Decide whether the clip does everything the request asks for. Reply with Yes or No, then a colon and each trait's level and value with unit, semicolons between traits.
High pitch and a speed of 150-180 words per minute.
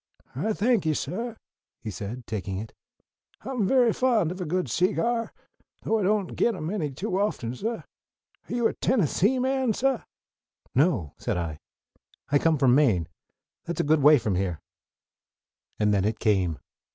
No: medium, 165 Hz; average, 165 wpm